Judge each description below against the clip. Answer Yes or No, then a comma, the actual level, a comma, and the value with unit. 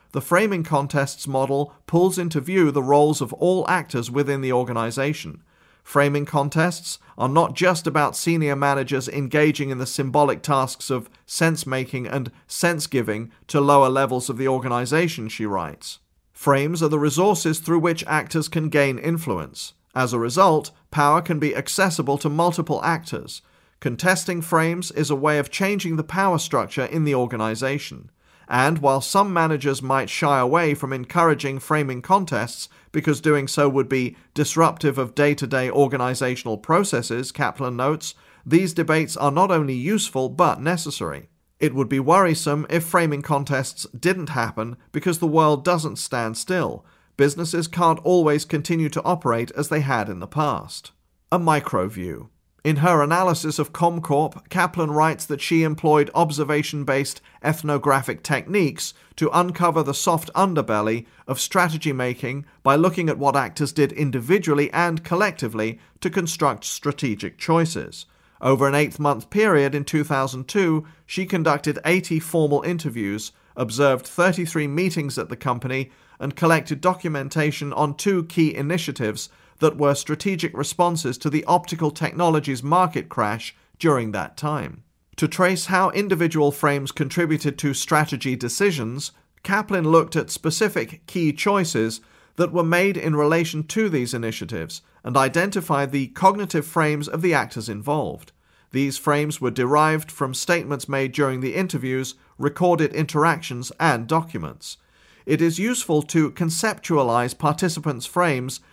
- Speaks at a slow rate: No, average, 145 wpm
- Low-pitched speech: No, medium, 150 Hz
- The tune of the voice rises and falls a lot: No, average, 3.8 semitones